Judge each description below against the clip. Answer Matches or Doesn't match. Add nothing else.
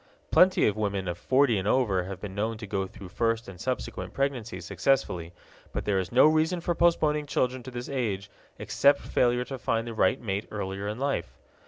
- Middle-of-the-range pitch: Doesn't match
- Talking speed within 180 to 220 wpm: Matches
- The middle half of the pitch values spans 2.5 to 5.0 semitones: Doesn't match